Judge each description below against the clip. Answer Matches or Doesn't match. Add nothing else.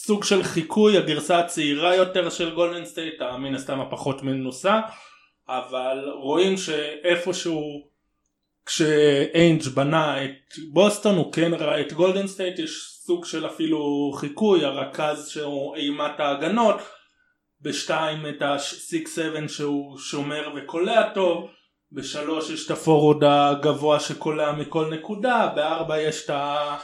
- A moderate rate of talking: Matches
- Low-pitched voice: Doesn't match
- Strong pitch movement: Doesn't match